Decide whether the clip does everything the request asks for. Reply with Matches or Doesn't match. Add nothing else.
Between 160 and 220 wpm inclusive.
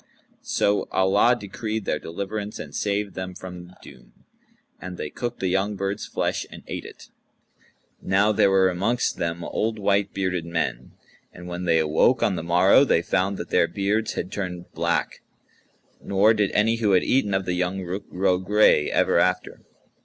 Matches